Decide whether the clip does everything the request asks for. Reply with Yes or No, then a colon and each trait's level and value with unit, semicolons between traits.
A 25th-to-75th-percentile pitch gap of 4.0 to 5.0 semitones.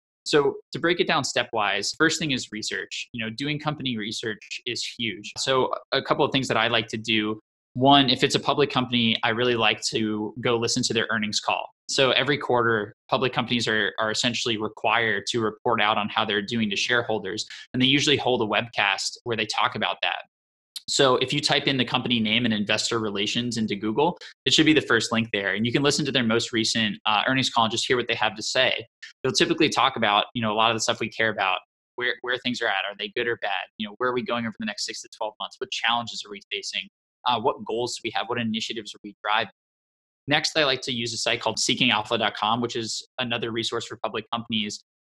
No: average, 3.3 semitones